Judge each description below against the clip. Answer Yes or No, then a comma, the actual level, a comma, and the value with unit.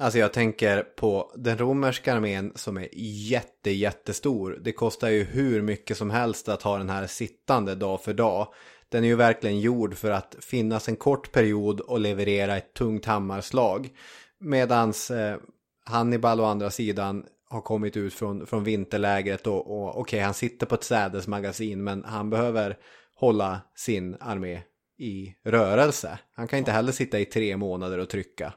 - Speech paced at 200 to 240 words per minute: No, average, 170 wpm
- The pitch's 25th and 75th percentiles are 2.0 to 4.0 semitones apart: Yes, narrow, 2.6 semitones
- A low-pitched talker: Yes, low, 105 Hz